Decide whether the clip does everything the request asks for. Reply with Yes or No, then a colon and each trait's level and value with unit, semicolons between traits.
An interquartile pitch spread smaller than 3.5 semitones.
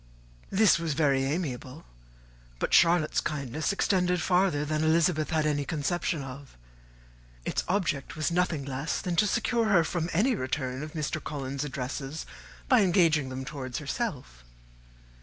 No: average, 4.2 semitones